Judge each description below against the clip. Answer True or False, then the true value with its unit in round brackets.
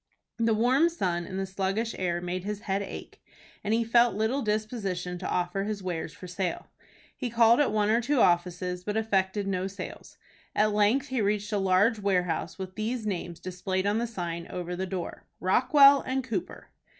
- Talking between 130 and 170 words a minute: False (185 wpm)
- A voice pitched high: True (200 Hz)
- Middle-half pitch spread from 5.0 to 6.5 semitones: False (3.5 semitones)